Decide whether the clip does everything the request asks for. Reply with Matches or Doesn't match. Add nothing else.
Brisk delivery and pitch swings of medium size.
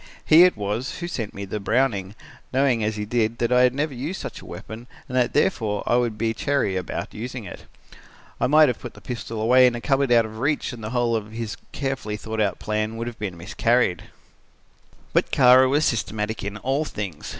Matches